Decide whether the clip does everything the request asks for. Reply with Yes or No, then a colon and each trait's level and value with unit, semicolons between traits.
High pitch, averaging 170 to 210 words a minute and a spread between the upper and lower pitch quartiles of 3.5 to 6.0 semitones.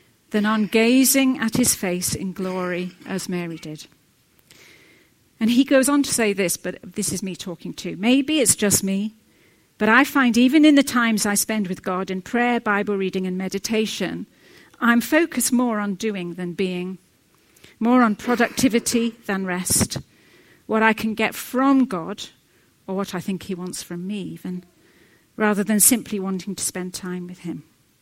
Yes: high, 205 Hz; average, 175 wpm; average, 4.3 semitones